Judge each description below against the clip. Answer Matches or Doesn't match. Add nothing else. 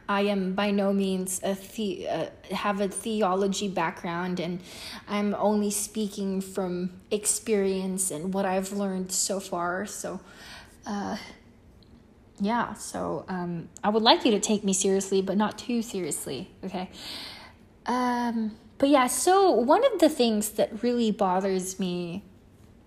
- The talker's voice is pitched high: Matches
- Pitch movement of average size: Doesn't match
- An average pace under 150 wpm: Matches